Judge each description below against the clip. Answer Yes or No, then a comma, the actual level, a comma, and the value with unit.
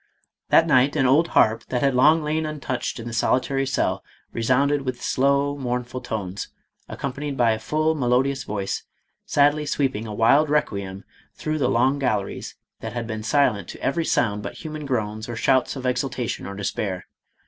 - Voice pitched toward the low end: Yes, low, 130 Hz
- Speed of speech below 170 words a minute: No, average, 175 wpm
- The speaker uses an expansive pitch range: No, average, 4.2 semitones